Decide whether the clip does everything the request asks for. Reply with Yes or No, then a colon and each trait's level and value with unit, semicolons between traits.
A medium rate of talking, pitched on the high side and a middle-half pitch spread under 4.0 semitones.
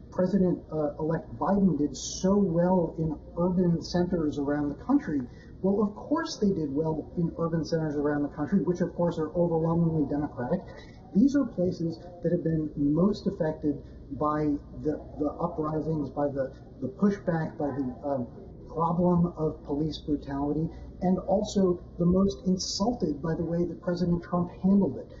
No: average, 160 wpm; medium, 165 Hz; average, 3.3 semitones